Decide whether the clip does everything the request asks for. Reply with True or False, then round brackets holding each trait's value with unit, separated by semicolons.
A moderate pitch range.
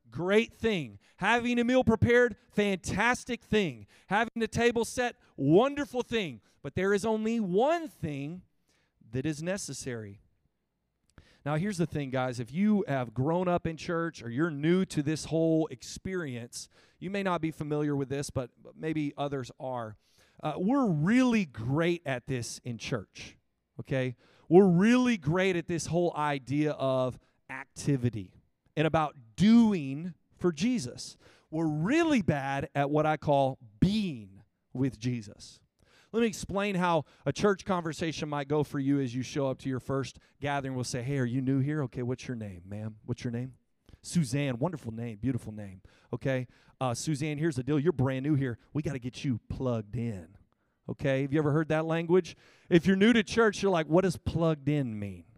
False (6.0 semitones)